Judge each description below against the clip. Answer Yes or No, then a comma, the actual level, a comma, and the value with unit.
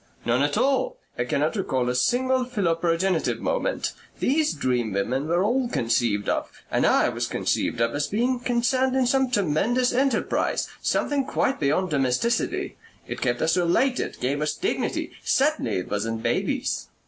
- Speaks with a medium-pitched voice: Yes, medium, 180 Hz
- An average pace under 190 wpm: Yes, average, 155 wpm